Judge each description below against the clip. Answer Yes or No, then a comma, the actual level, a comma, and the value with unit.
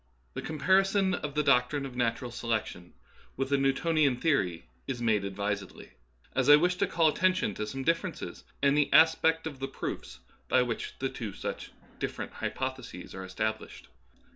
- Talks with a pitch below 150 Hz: Yes, low, 135 Hz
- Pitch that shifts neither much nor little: No, wide, 6.0 semitones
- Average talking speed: Yes, average, 165 wpm